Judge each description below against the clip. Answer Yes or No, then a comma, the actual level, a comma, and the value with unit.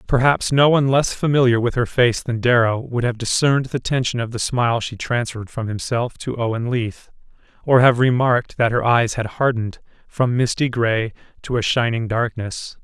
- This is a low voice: Yes, low, 120 Hz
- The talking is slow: No, average, 185 wpm